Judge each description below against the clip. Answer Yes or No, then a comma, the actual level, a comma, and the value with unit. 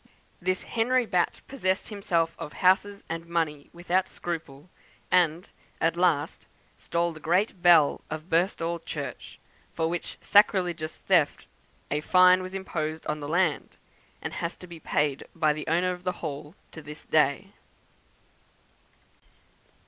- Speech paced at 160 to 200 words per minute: No, average, 140 wpm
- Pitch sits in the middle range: Yes, medium, 170 Hz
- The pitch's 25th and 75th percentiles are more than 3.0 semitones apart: No, average, 2.7 semitones